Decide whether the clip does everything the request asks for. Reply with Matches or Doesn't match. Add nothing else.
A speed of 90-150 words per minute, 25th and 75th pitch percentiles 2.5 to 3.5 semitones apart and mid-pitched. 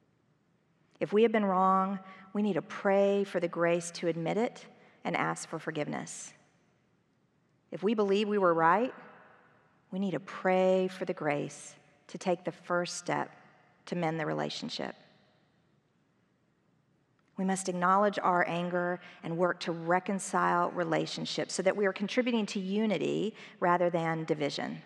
Matches